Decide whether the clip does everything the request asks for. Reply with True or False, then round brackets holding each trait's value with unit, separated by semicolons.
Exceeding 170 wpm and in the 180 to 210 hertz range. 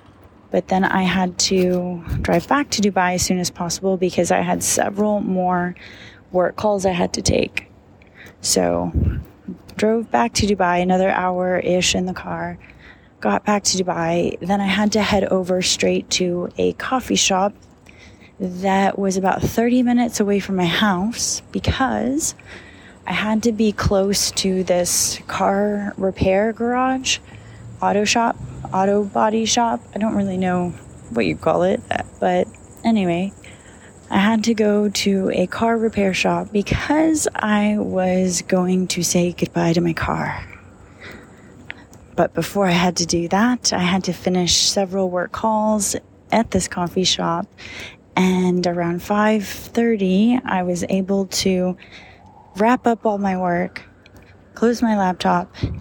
False (145 wpm; 185 Hz)